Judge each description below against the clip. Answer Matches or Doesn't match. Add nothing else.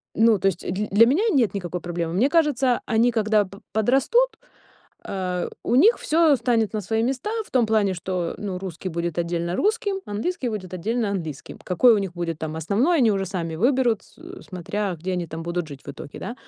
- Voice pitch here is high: Matches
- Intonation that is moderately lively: Doesn't match